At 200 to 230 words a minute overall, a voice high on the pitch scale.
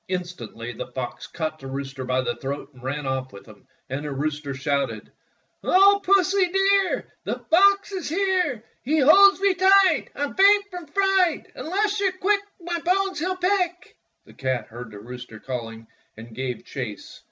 No: average, 185 wpm; very high, 260 Hz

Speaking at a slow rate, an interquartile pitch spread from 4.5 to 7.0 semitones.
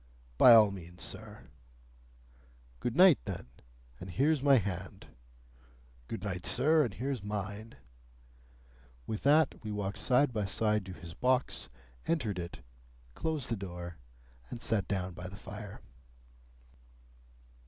Yes: slow, 130 wpm; average, 5.2 semitones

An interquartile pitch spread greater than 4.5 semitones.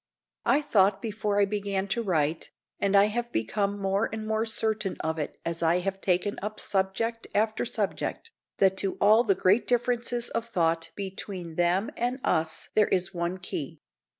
No: average, 3.2 semitones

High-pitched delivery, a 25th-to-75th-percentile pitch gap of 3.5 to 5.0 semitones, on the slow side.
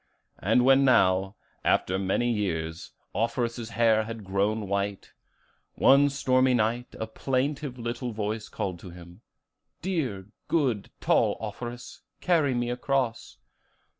No: low, 115 Hz; average, 4.4 semitones; slow, 120 wpm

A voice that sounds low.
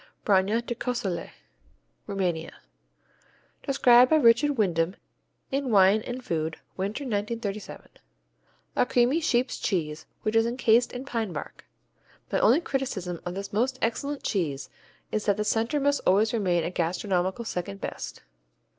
No: high, 215 Hz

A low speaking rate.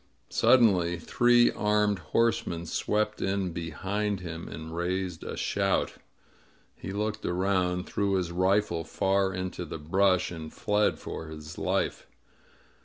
Yes: slow, 125 wpm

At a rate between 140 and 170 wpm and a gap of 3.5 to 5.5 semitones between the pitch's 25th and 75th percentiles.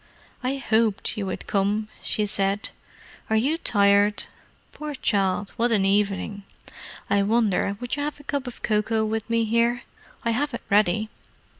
No: average, 160 wpm; average, 2.9 semitones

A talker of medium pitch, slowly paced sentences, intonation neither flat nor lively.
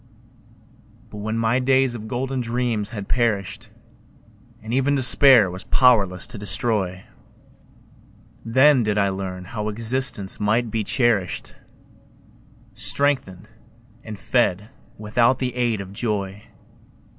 No: low, 110 Hz; slow, 115 wpm; average, 3.4 semitones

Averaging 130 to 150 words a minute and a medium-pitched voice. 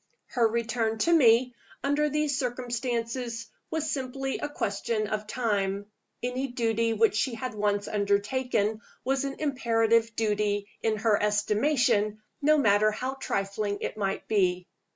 No: slow, 135 wpm; high, 230 Hz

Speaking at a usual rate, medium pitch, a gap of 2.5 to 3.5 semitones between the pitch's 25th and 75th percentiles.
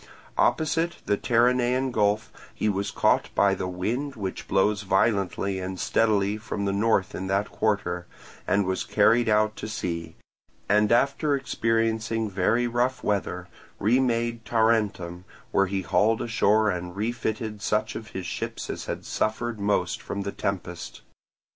No: average, 145 wpm; low, 105 Hz; average, 2.9 semitones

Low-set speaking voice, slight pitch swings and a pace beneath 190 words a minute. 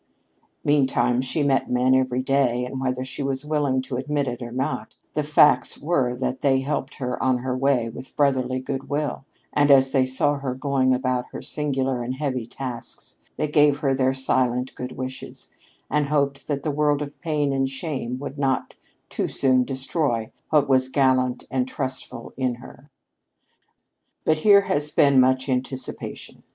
Yes: low, 130 Hz; narrow, 1.8 semitones; average, 170 wpm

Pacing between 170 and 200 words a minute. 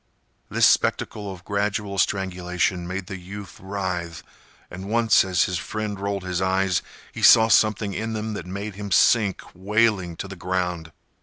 No: average, 160 wpm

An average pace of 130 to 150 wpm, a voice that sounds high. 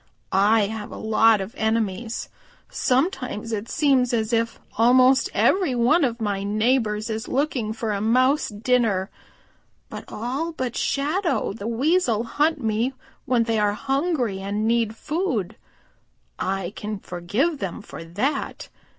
Yes: average, 140 wpm; high, 230 Hz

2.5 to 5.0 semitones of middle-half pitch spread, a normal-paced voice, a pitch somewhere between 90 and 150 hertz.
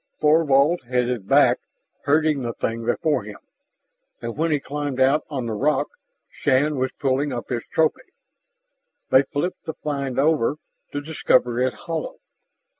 Yes: average, 3.3 semitones; average, 145 wpm; medium, 140 Hz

